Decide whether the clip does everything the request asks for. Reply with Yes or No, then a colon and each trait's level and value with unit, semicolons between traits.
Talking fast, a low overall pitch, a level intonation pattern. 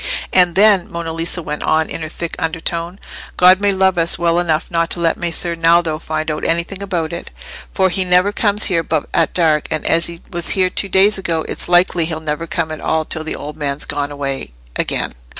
No: fast, 220 wpm; medium, 170 Hz; narrow, 2.3 semitones